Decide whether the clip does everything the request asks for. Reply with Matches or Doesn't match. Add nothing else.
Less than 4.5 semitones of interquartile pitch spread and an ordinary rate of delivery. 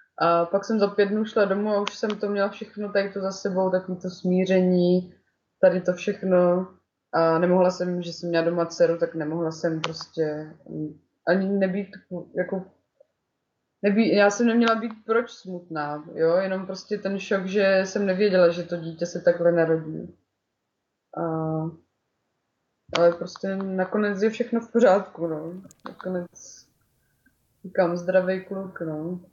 Matches